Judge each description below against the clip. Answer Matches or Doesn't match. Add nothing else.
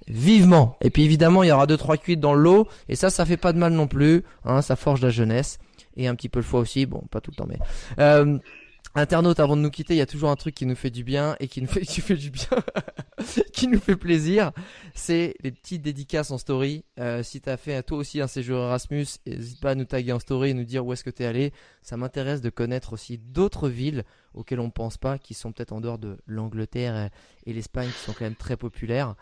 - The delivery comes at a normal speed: Doesn't match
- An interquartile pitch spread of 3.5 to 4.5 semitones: Matches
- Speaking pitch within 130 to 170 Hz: Matches